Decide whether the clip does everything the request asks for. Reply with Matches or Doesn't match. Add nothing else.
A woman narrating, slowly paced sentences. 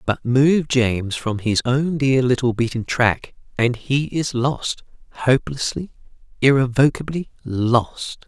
Doesn't match